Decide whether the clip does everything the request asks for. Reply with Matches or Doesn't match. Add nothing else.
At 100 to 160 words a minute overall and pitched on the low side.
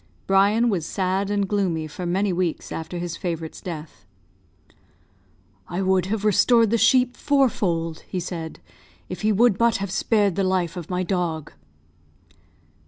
Doesn't match